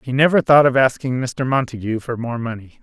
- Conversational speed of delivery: No, fast, 210 wpm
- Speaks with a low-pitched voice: Yes, low, 125 Hz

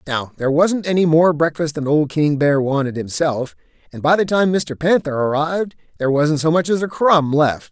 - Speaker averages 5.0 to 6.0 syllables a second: Yes, 5.2 syllables/s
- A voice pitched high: No, medium, 155 Hz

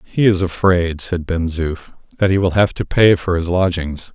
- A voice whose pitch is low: Yes, very low, 90 Hz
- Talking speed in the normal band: No, fast, 215 wpm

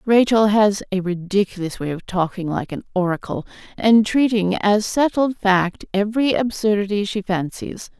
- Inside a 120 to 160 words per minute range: Yes, average, 145 wpm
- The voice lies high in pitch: Yes, high, 205 Hz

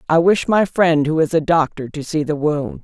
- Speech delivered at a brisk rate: Yes, fast, 255 wpm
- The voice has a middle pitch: Yes, medium, 160 Hz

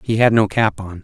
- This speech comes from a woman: No, male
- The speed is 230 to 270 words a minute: No, fast, 290 wpm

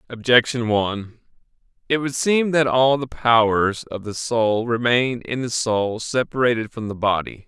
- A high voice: No, low, 120 Hz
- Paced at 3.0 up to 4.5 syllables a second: Yes, 4.4 syllables/s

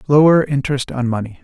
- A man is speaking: Yes, male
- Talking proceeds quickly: No, average, 170 wpm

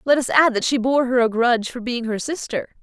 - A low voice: No, high, 245 Hz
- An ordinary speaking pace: No, fast, 275 wpm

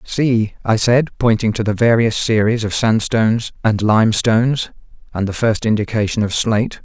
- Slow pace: No, average, 160 wpm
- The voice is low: Yes, low, 110 Hz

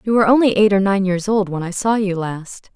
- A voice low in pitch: No, high, 200 Hz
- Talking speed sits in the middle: No, fast, 285 wpm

